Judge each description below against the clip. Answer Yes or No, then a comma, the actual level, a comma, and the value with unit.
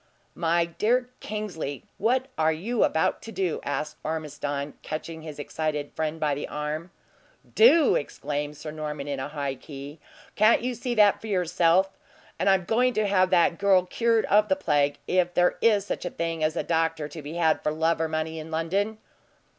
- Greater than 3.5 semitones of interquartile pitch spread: Yes, average, 4.7 semitones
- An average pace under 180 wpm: No, average, 185 wpm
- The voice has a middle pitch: Yes, medium, 165 Hz